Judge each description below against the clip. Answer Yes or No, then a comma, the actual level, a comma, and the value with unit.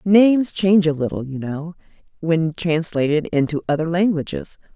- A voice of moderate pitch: Yes, medium, 165 Hz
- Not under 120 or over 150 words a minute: Yes, average, 140 wpm